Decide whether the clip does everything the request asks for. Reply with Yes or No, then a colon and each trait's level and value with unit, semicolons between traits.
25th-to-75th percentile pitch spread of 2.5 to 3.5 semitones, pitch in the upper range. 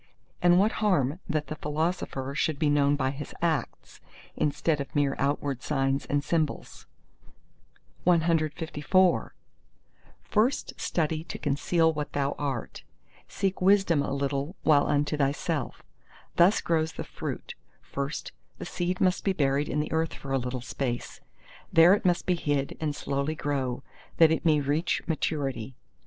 No: average, 3.1 semitones; medium, 150 Hz